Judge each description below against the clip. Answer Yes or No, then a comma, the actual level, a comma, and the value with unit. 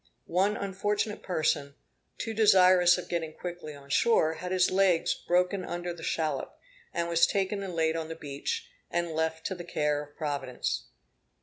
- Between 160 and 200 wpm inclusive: Yes, average, 170 wpm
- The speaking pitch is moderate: Yes, medium, 175 Hz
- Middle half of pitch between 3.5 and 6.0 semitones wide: No, average, 2.8 semitones